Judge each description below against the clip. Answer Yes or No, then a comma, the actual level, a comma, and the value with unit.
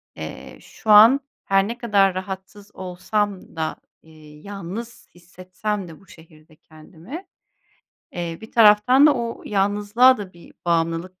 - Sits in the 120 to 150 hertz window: No, high, 195 Hz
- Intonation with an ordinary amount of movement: Yes, average, 3.8 semitones